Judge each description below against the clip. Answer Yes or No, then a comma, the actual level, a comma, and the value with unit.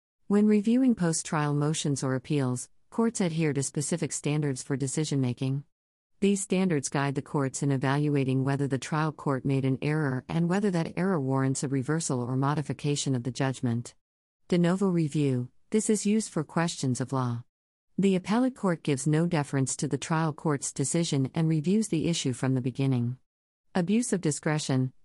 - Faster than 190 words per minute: No, average, 170 wpm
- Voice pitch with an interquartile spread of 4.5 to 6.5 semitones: No, average, 4.1 semitones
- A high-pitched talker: No, medium, 145 Hz